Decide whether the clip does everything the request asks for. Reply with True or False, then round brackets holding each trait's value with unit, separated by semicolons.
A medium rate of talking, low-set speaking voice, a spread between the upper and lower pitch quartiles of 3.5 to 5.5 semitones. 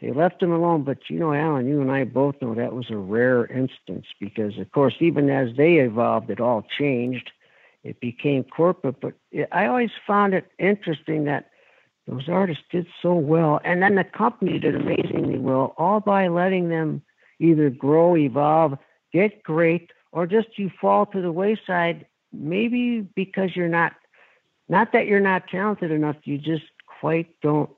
False (175 wpm; 160 Hz; 4.7 semitones)